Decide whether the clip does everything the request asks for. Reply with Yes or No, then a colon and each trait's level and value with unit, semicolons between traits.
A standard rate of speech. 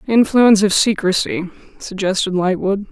No: slow, 105 wpm